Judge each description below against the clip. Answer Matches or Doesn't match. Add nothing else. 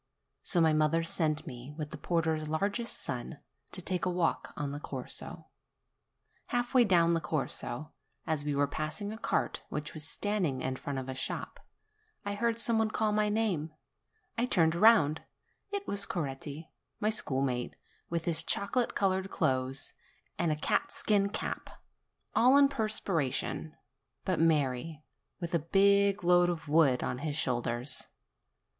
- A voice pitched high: Doesn't match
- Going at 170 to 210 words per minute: Doesn't match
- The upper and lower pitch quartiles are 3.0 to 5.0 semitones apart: Doesn't match